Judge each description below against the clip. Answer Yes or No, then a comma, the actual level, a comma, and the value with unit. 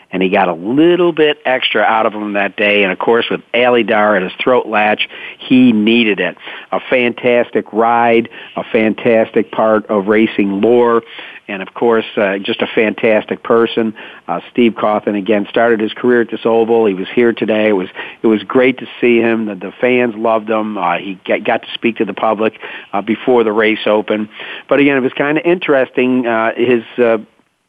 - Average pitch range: No, narrow, 2.1 semitones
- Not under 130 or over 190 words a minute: No, average, 200 wpm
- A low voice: Yes, low, 115 Hz